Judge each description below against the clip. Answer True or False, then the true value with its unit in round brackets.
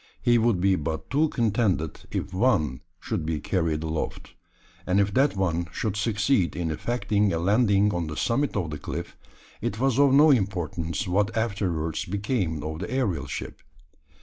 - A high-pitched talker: False (100 Hz)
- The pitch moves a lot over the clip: True (5.9 semitones)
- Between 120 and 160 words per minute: False (170 wpm)